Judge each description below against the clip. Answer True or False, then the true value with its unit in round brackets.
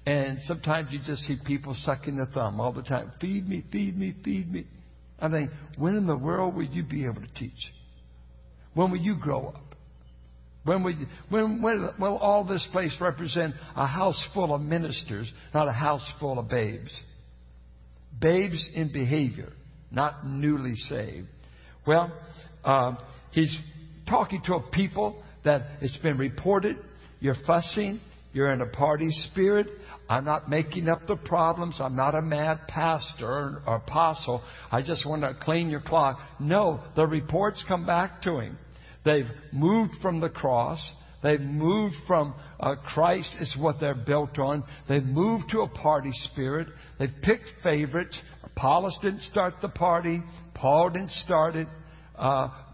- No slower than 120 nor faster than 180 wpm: True (160 wpm)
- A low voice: False (155 Hz)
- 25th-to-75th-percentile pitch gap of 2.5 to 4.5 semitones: True (4.0 semitones)